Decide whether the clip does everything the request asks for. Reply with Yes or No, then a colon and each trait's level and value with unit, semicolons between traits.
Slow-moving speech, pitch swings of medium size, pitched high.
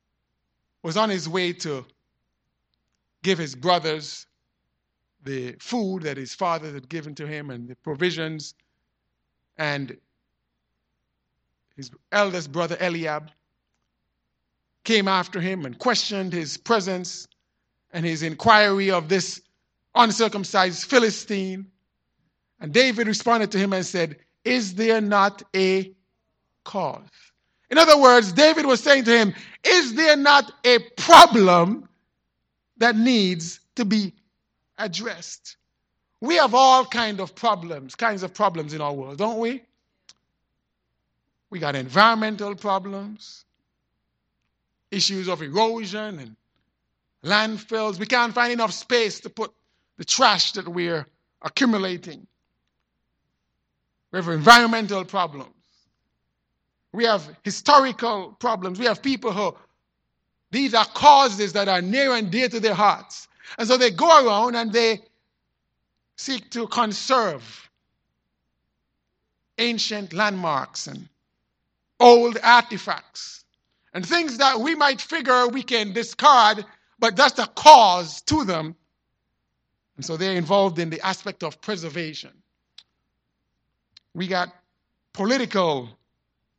No: slow, 115 wpm; wide, 6.1 semitones; high, 195 Hz